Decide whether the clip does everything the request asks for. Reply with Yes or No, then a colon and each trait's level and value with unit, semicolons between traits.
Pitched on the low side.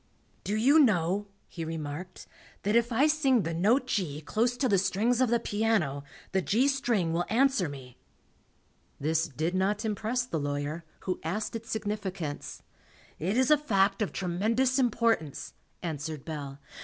No: high, 200 Hz